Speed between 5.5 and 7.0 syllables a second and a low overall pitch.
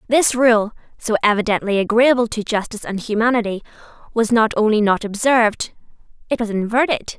No: 5.7 syllables/s; high, 225 Hz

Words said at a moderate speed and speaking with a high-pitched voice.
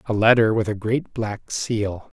No: average, 190 wpm; low, 110 Hz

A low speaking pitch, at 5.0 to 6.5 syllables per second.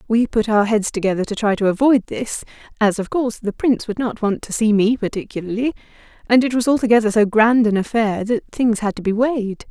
No: high, 220 Hz; 5.8 syllables/s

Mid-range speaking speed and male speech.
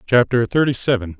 Yes: average, 150 wpm; male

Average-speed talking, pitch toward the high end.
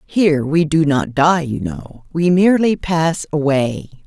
No: average, 160 wpm; medium, 160 Hz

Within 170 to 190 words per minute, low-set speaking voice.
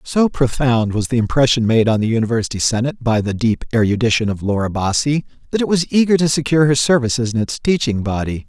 No: fast, 205 wpm; low, 125 Hz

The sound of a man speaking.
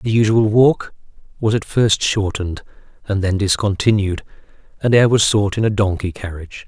Yes: male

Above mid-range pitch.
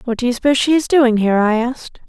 Yes: high, 245 Hz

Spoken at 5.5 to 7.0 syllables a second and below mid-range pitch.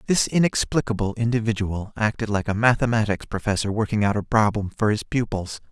Yes: 5.7 syllables/s; low, 110 Hz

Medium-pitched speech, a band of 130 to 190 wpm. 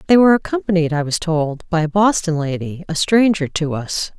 No: medium, 170 Hz; average, 200 wpm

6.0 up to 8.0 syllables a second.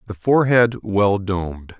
No: 4.6 syllables/s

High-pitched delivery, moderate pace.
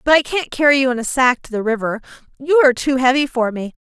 No: very high, 260 Hz; fast, 265 wpm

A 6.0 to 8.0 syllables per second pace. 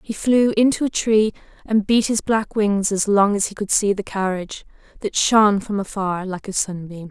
No: 4.9 syllables/s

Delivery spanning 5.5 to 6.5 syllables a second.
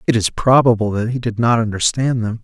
Yes: 5.7 syllables/s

